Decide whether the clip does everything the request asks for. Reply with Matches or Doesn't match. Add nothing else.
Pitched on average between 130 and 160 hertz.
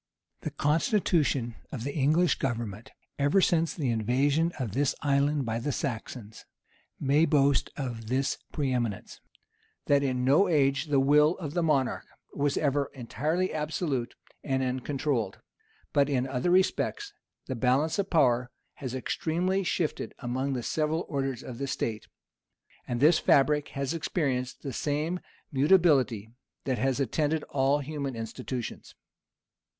Matches